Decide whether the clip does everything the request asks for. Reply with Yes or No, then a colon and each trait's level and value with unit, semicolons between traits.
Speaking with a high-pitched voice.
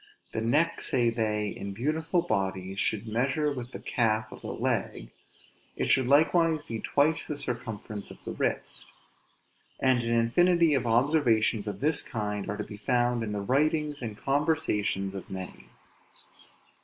No: low, 120 Hz